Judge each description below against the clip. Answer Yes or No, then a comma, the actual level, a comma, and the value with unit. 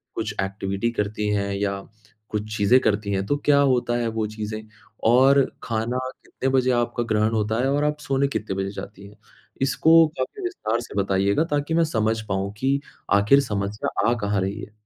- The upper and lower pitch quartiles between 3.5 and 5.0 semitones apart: Yes, average, 4.3 semitones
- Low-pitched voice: Yes, low, 110 Hz